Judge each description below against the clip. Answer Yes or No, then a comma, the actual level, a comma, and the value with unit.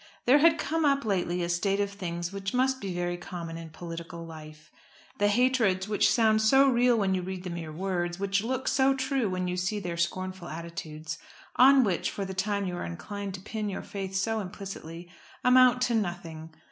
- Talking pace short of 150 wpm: No, average, 200 wpm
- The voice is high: Yes, high, 195 Hz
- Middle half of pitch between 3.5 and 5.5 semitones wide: Yes, average, 4.5 semitones